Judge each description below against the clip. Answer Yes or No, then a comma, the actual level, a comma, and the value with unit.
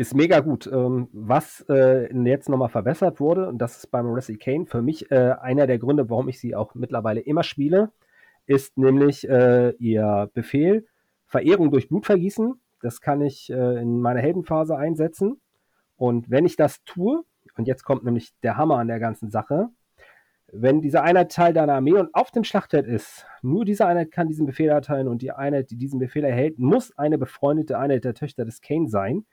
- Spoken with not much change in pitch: No, average, 4.6 semitones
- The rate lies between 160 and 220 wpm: Yes, fast, 190 wpm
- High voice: No, medium, 140 Hz